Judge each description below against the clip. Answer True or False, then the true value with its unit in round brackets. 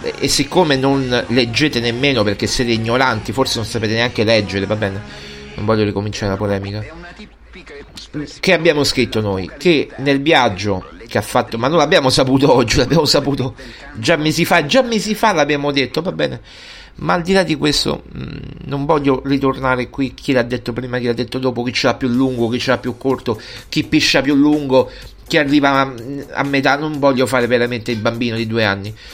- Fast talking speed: True (190 wpm)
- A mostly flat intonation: False (3.8 semitones)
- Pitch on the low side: True (130 Hz)